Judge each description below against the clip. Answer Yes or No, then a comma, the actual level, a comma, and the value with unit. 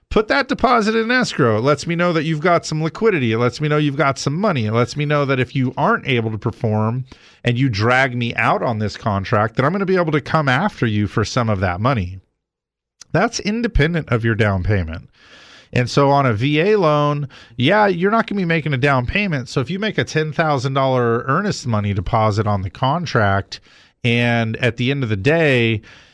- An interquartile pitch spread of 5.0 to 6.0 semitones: Yes, wide, 5.6 semitones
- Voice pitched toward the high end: No, low, 135 Hz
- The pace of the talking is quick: Yes, fast, 225 wpm